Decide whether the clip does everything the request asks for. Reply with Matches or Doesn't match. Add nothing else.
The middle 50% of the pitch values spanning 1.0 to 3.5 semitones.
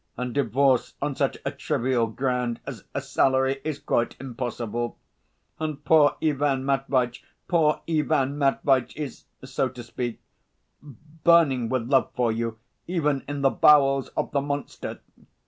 Matches